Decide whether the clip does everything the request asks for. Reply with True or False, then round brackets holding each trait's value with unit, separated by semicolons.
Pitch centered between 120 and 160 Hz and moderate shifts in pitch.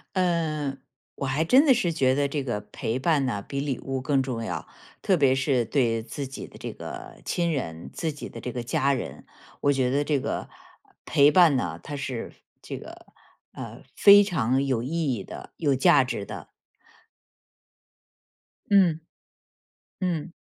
True (140 Hz; 3.8 semitones)